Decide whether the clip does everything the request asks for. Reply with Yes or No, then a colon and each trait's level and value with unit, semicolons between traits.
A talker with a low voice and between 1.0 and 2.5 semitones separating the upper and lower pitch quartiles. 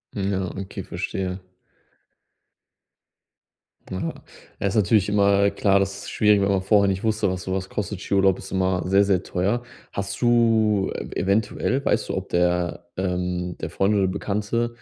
Yes: low, 100 Hz; narrow, 1.8 semitones